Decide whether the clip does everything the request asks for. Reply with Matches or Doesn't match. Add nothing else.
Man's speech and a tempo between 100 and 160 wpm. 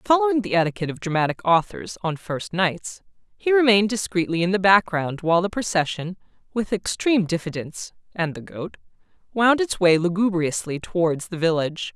Matches